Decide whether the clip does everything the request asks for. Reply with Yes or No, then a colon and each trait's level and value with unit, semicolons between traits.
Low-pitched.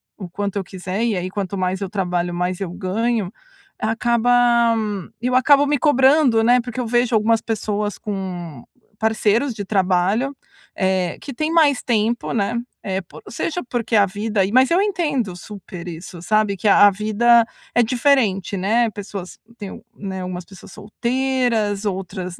No: high, 215 Hz